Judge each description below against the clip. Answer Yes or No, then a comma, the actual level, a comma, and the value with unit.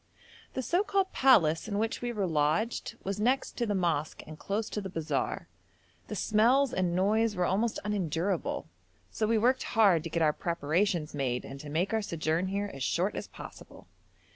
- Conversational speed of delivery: Yes, average, 190 wpm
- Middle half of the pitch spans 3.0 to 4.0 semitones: No, wide, 5.4 semitones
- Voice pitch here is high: Yes, high, 195 Hz